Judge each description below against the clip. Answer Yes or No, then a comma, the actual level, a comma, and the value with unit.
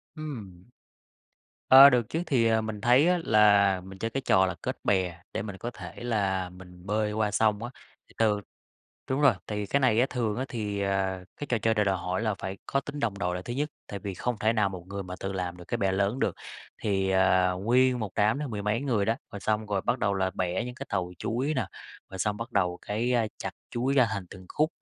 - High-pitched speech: No, low, 105 Hz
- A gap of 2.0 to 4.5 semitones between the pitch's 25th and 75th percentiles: Yes, average, 3.9 semitones